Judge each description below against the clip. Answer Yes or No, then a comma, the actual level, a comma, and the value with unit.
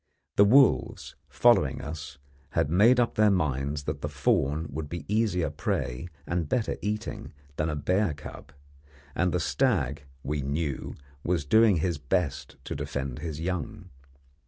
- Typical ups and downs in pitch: No, wide, 5.7 semitones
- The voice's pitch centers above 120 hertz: No, very low, 80 Hz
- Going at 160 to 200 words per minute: No, average, 150 wpm